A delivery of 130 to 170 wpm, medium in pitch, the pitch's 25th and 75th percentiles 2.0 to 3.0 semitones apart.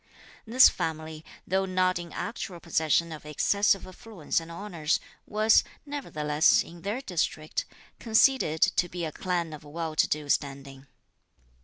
No: average, 140 wpm; medium, 170 Hz; average, 3.9 semitones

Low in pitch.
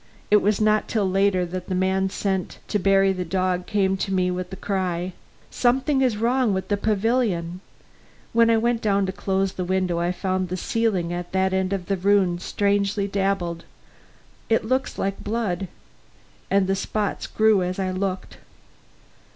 No: high, 195 Hz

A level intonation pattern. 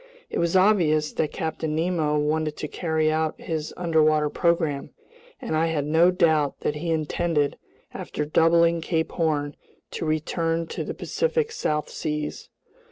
Yes: narrow, 1.9 semitones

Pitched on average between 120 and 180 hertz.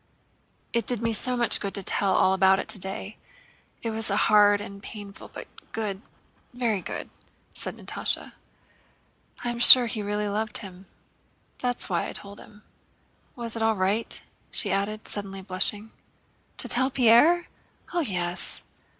No: high, 210 Hz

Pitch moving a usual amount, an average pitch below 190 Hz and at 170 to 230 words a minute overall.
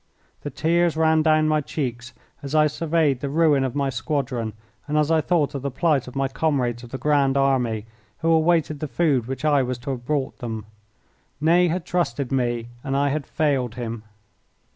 Yes: average, 3.6 semitones; medium, 140 Hz; average, 195 wpm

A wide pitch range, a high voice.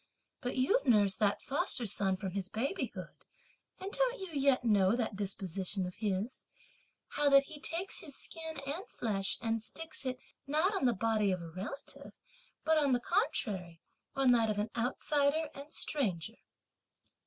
Yes: wide, 6.6 semitones; high, 245 Hz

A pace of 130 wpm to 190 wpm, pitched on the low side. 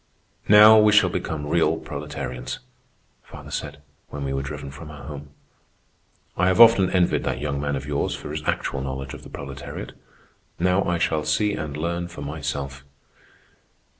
Yes: average, 165 wpm; very low, 75 Hz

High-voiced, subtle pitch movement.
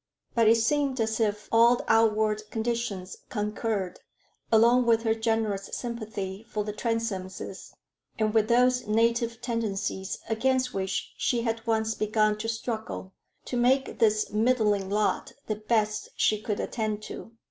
Yes: high, 220 Hz; narrow, 1.7 semitones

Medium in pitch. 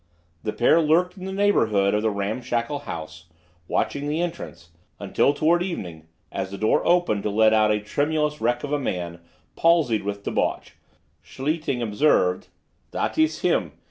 No: low, 120 Hz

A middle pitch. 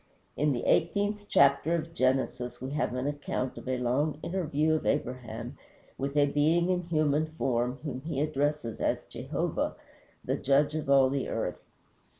Yes: medium, 145 Hz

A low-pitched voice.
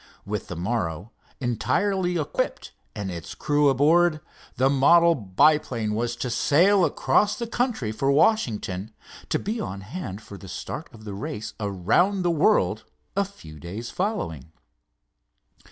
Yes: low, 125 Hz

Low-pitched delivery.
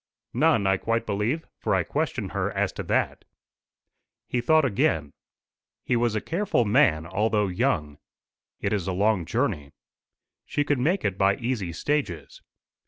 Yes: low, 105 Hz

